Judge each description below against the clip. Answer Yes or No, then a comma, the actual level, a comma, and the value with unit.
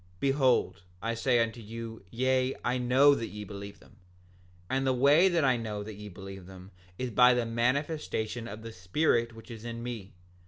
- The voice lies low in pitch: Yes, low, 115 Hz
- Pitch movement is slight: No, average, 3.4 semitones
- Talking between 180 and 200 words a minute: Yes, average, 190 wpm